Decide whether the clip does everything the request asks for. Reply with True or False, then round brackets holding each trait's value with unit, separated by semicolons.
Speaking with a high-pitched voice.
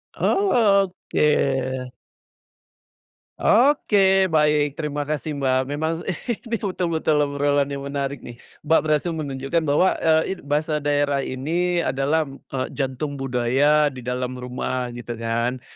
False (145 Hz)